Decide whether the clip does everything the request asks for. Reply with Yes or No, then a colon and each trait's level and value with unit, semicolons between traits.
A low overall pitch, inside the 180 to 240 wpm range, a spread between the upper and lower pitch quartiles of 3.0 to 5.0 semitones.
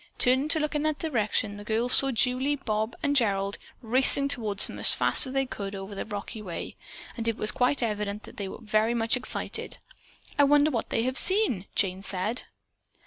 No: high, 230 Hz; fast, 205 wpm; average, 4.6 semitones